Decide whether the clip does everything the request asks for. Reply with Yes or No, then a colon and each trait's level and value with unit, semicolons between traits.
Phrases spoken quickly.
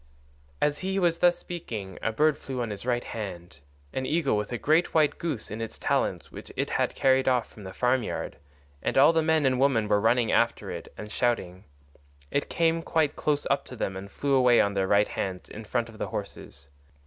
Yes: fast, 210 wpm